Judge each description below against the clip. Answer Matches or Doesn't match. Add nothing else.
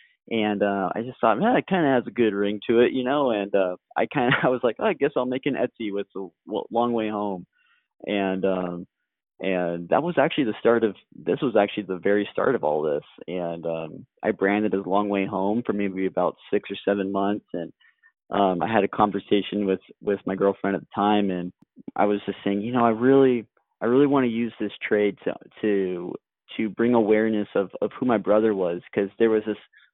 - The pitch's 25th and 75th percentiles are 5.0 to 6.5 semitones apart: Doesn't match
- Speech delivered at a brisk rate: Matches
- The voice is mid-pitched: Doesn't match